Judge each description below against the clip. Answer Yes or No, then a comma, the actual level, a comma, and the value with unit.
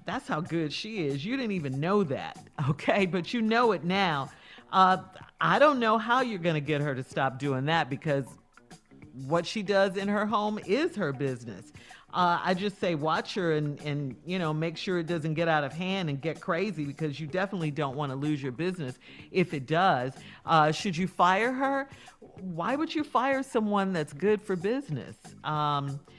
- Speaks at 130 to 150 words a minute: No, average, 200 wpm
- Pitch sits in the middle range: Yes, medium, 170 Hz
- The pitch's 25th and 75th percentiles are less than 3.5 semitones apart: No, average, 5.2 semitones